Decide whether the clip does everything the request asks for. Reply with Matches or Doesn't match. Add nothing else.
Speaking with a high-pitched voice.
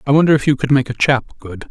Doesn't match